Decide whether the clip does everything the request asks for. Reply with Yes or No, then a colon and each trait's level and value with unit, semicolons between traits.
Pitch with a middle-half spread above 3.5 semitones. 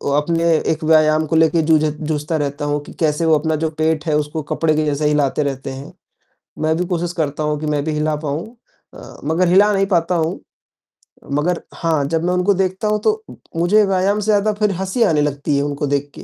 No: average, 3.1 semitones